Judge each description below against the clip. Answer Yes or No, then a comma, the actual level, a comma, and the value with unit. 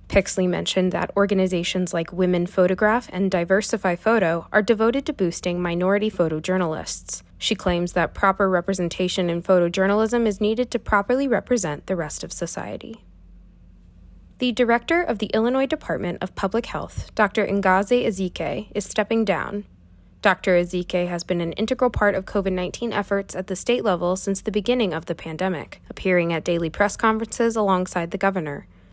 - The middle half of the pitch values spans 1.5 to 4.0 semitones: Yes, average, 3.6 semitones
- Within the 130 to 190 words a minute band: Yes, average, 155 wpm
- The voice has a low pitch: No, high, 190 Hz